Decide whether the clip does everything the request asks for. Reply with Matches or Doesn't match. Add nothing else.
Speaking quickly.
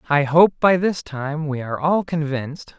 Doesn't match